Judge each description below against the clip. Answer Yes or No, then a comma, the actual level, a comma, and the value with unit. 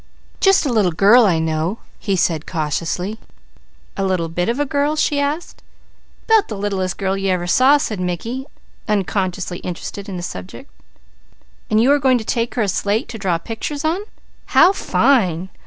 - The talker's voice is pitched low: No, high, 200 Hz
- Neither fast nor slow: Yes, average, 175 wpm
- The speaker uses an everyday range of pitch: No, wide, 6.2 semitones